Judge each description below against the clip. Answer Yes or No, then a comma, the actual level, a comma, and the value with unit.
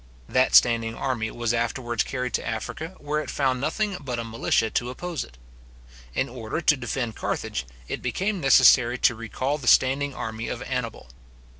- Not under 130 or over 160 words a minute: No, average, 170 wpm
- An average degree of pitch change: Yes, average, 3.6 semitones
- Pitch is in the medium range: No, low, 125 Hz